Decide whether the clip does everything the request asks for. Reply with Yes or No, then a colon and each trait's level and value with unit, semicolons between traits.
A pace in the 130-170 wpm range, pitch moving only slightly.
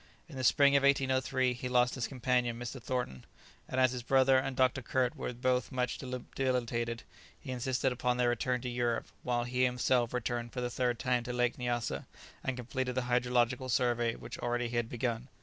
No: average, 195 wpm; narrow, 1.2 semitones